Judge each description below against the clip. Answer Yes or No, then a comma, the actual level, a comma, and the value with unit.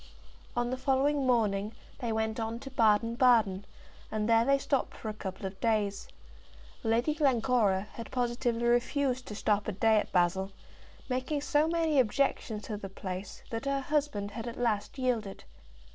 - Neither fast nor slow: Yes, average, 170 wpm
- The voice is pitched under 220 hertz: No, high, 230 Hz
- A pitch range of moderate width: Yes, average, 3.7 semitones